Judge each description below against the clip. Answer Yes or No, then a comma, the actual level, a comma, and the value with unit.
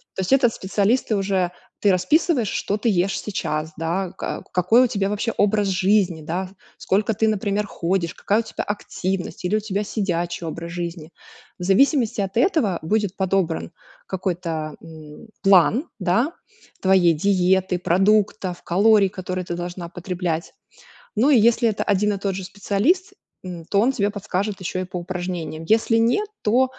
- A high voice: Yes, high, 195 Hz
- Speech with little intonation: No, average, 3.2 semitones